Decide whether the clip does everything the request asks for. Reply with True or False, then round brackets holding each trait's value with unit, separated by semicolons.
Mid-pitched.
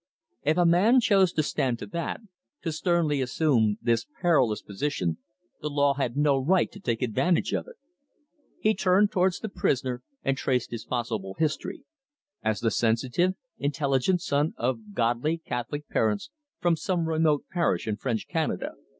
True (145 Hz)